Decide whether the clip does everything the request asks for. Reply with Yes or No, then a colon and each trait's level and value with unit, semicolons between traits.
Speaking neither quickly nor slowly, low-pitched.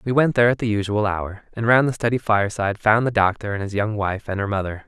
No: fast, 270 wpm; low, 105 Hz